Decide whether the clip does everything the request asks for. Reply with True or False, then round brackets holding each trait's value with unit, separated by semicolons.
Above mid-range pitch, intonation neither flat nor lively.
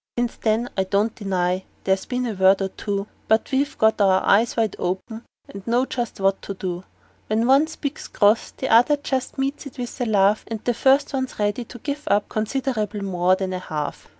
True (220 Hz; 4.4 semitones)